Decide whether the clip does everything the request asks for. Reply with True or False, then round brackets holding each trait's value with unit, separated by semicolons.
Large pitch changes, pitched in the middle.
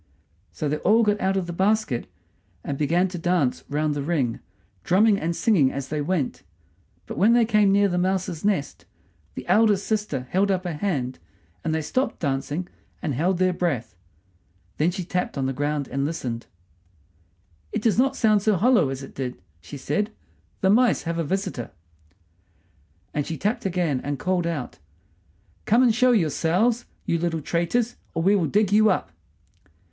True (5.8 semitones; 175 Hz)